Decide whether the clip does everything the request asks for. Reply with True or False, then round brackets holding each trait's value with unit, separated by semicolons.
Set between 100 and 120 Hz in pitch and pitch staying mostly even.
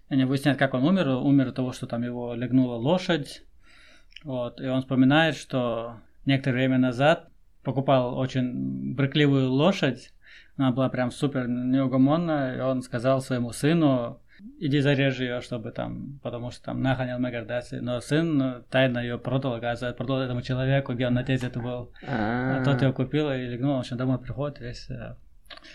False (130 Hz; 2.0 semitones)